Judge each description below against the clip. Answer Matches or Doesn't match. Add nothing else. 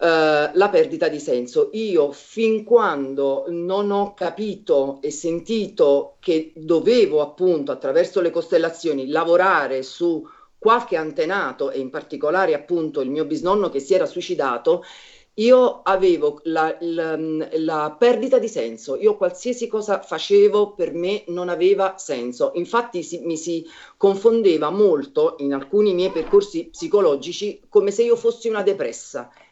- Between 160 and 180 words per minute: Doesn't match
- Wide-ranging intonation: Matches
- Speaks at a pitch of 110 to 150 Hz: Doesn't match